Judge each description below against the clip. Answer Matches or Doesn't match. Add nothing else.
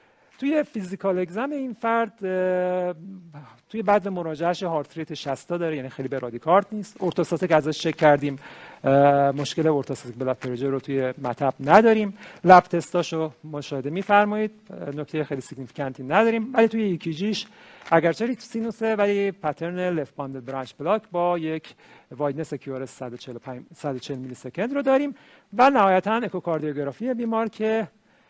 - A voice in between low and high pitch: Matches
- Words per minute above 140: Doesn't match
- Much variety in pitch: Matches